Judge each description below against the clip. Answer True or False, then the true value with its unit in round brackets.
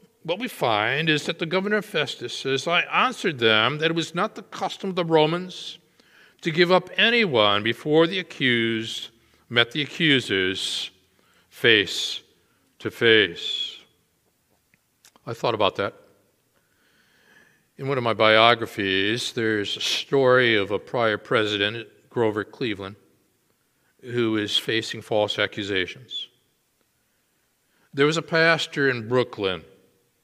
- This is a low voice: True (125 Hz)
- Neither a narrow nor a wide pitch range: False (6.9 semitones)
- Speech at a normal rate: False (125 wpm)